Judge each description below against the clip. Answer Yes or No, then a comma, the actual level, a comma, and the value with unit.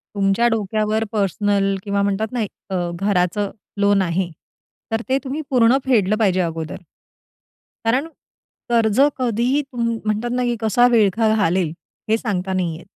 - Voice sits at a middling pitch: No, high, 210 Hz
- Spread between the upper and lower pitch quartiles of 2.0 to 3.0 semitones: No, average, 3.4 semitones